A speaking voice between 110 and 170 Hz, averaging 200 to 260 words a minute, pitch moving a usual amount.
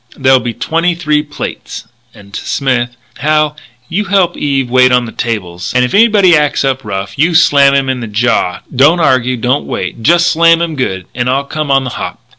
Yes: low, 135 Hz; fast, 205 wpm; average, 4.4 semitones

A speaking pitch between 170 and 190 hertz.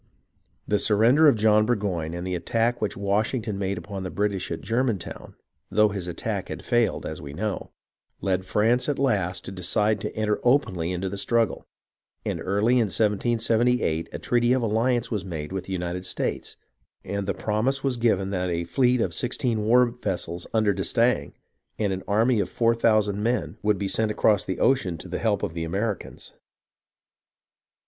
No: low, 105 Hz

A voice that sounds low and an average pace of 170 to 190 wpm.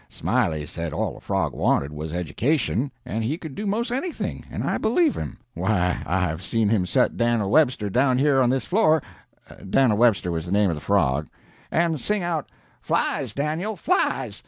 Yes: low, 120 Hz; average, 180 wpm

